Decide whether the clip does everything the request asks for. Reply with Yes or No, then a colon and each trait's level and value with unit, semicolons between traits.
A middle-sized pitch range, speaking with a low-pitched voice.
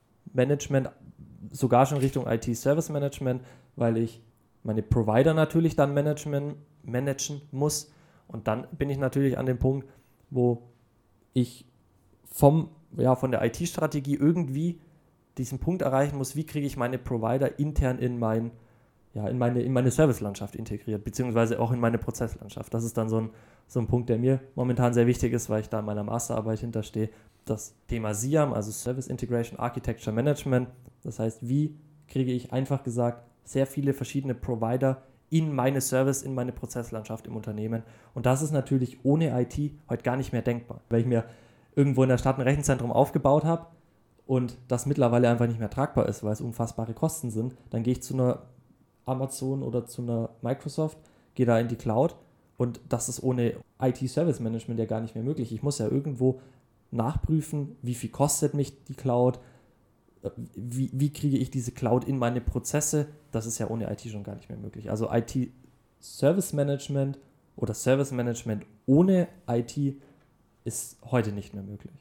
Yes: average, 3.1 semitones; low, 125 Hz